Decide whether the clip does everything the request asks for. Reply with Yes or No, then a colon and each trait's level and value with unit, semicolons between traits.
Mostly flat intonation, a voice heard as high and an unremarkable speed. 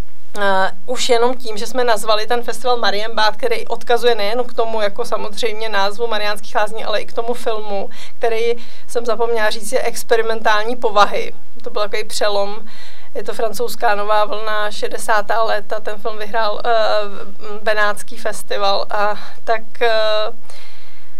Yes: narrow, 2.0 semitones; high, 220 Hz; average, 150 wpm